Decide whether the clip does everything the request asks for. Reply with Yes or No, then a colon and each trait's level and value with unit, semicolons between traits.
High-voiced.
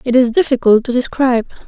Yes: high, 245 Hz